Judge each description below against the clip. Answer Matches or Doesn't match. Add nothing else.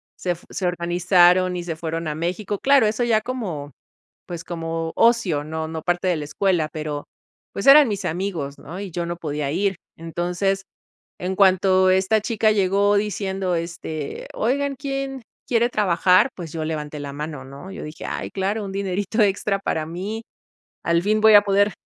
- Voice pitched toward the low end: Doesn't match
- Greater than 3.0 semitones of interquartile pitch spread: Matches